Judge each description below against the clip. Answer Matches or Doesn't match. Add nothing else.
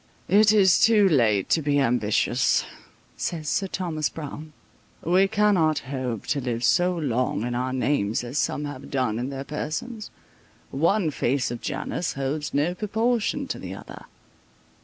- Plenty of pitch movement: Matches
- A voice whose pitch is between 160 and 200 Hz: Doesn't match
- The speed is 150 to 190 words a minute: Matches